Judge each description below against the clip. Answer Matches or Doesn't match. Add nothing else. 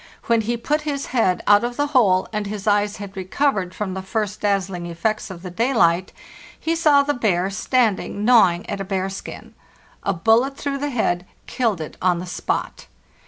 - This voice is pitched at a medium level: Doesn't match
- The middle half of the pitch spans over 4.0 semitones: Matches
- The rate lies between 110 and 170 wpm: Doesn't match